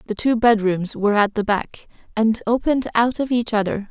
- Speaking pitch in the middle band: No, high, 220 Hz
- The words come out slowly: No, average, 200 wpm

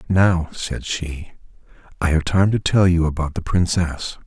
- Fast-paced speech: No, average, 170 wpm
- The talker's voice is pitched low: Yes, very low, 85 Hz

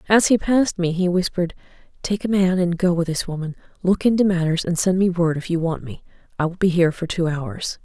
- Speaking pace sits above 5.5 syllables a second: Yes, 5.9 syllables/s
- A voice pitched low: No, medium, 180 Hz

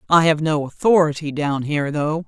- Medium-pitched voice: Yes, medium, 155 Hz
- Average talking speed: Yes, average, 185 wpm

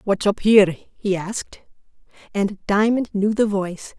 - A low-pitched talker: No, high, 200 Hz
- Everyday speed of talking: Yes, average, 150 wpm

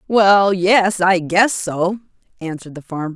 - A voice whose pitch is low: No, medium, 185 Hz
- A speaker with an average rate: Yes, average, 150 wpm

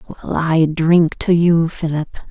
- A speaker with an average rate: Yes, average, 155 wpm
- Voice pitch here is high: No, medium, 165 Hz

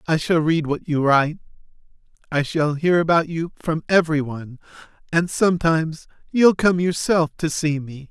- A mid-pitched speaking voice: Yes, medium, 160 Hz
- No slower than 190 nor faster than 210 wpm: No, average, 155 wpm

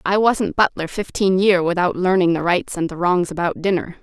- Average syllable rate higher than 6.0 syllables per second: No, 5.1 syllables/s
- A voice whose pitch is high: No, medium, 180 Hz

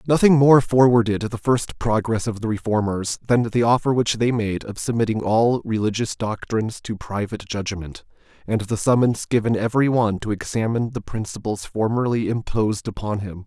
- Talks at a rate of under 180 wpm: Yes, average, 165 wpm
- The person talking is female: No, male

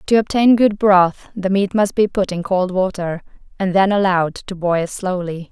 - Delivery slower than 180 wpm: No, average, 195 wpm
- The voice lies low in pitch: No, high, 190 Hz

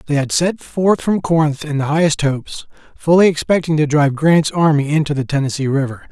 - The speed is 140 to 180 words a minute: No, average, 195 wpm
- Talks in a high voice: No, medium, 150 Hz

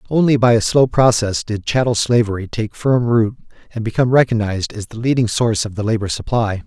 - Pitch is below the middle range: Yes, low, 115 Hz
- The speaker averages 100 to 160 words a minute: No, average, 200 wpm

